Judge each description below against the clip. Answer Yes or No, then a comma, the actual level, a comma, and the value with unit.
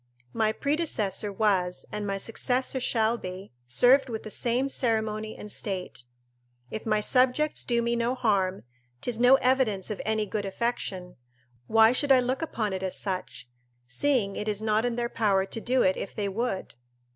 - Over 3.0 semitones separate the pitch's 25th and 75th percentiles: Yes, average, 3.7 semitones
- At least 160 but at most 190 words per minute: Yes, average, 175 wpm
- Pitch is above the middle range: Yes, high, 220 Hz